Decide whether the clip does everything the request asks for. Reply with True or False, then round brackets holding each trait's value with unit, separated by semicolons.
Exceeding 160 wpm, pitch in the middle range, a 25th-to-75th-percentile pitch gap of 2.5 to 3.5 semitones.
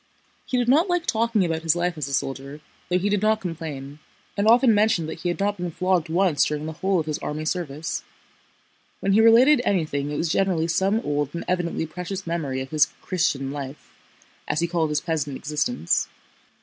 False (200 wpm; 170 Hz; 4.5 semitones)